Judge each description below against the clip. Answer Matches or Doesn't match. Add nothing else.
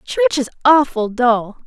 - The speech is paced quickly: Doesn't match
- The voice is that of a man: Doesn't match